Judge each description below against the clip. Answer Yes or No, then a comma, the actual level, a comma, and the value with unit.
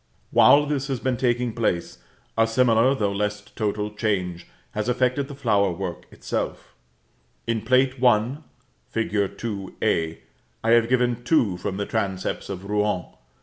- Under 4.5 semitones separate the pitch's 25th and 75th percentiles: Yes, average, 3.8 semitones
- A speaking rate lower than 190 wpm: Yes, average, 145 wpm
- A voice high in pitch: No, low, 110 Hz